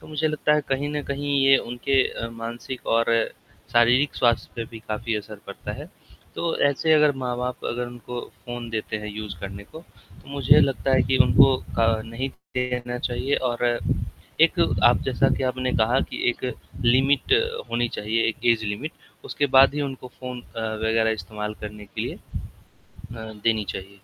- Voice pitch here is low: Yes, low, 120 Hz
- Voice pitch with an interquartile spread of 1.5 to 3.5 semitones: Yes, average, 3.1 semitones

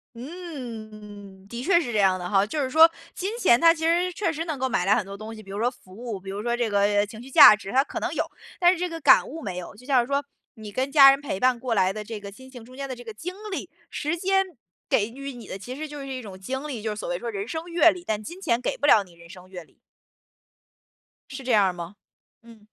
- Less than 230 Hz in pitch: No, high, 240 Hz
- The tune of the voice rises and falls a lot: Yes, wide, 5.9 semitones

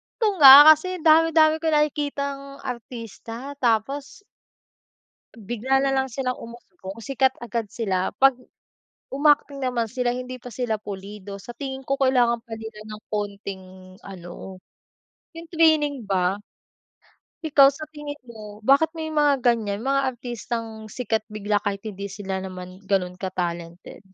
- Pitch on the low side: No, high, 240 Hz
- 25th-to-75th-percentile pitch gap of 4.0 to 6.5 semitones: Yes, average, 5.1 semitones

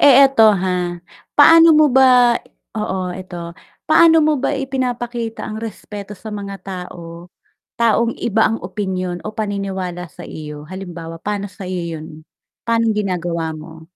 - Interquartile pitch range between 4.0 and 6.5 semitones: Yes, average, 4.6 semitones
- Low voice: No, high, 195 Hz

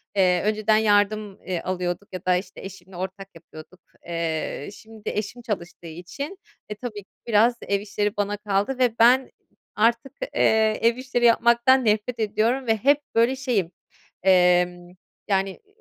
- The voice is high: Yes, high, 210 Hz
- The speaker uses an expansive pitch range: No, average, 4.0 semitones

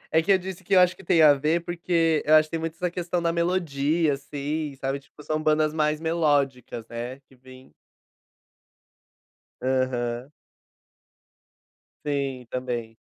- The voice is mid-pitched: Yes, medium, 150 Hz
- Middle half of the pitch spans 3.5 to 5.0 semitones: Yes, average, 4.0 semitones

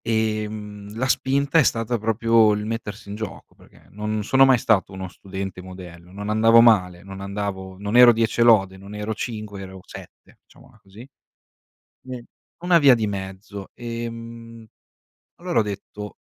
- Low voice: Yes, low, 105 Hz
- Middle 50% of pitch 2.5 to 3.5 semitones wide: Yes, average, 2.9 semitones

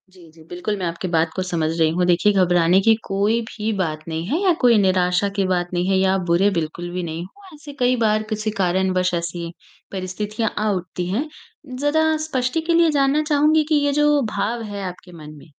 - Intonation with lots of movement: Yes, wide, 5.8 semitones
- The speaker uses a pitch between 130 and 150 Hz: No, high, 190 Hz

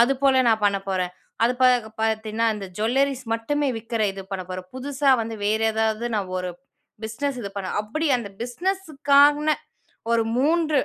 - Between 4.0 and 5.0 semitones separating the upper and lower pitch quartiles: Yes, average, 4.6 semitones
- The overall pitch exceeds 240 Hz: No, high, 235 Hz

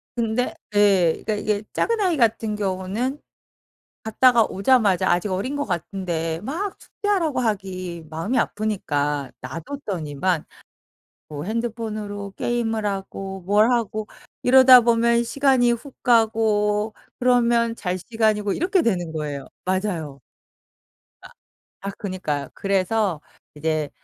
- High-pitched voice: Yes, high, 210 Hz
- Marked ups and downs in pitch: No, average, 4.3 semitones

